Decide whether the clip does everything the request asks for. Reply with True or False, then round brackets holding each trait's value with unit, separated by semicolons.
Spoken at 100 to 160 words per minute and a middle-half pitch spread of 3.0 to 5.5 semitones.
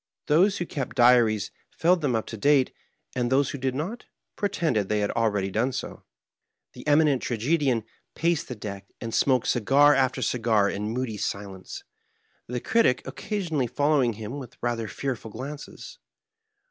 True (155 wpm; 4.7 semitones)